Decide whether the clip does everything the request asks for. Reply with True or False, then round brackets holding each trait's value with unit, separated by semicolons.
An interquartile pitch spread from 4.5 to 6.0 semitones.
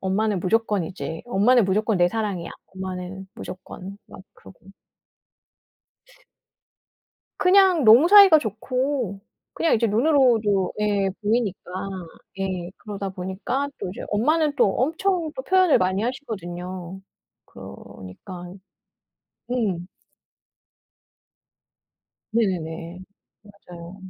True (5.3 semitones)